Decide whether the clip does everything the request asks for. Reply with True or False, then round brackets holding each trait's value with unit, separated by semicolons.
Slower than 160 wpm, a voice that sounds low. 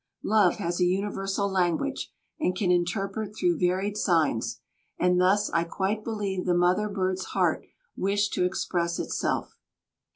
False (140 wpm; 185 Hz)